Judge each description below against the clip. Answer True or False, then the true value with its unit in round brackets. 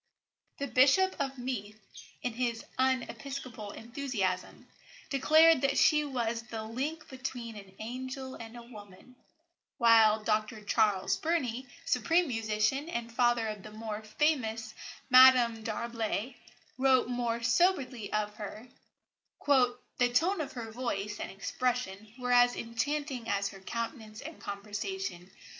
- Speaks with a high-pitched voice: True (235 Hz)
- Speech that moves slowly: True (125 wpm)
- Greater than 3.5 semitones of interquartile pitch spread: False (3.2 semitones)